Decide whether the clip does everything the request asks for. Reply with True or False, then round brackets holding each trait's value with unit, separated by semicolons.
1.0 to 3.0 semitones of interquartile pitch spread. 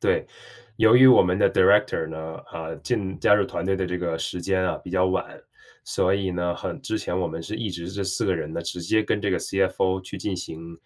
True (2.4 semitones)